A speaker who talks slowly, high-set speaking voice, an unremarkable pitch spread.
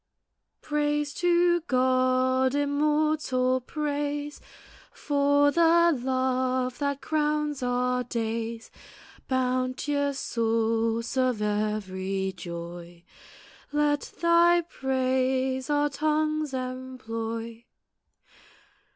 Yes: slow, 75 wpm; very high, 260 Hz; average, 3.7 semitones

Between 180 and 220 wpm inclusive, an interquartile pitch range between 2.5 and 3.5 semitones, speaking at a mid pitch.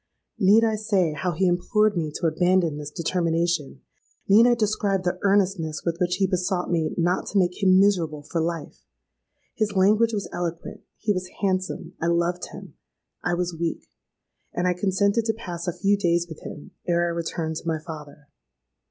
No: average, 170 wpm; average, 2.9 semitones; medium, 180 Hz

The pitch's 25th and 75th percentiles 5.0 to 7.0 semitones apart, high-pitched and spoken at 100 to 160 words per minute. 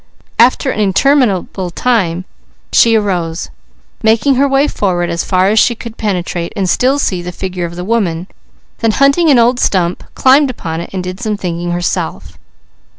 No: wide, 5.6 semitones; high, 200 Hz; average, 170 wpm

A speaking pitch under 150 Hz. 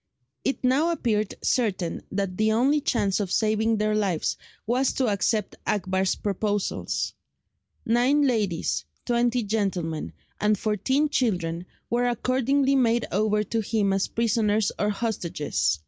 No: high, 215 Hz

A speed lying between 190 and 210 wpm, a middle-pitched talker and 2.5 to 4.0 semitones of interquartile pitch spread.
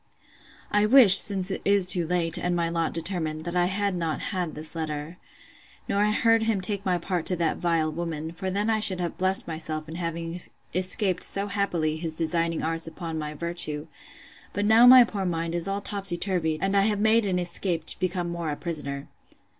Yes: average, 200 wpm; medium, 175 Hz; average, 3.2 semitones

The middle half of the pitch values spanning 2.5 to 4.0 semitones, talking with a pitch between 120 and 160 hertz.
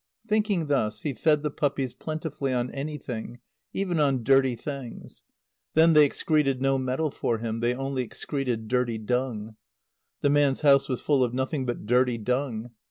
Yes: average, 3.2 semitones; low, 135 Hz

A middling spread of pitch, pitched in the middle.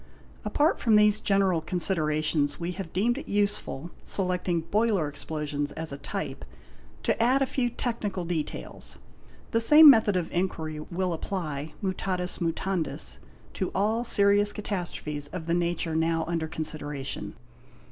Yes: average, 4.4 semitones; medium, 180 Hz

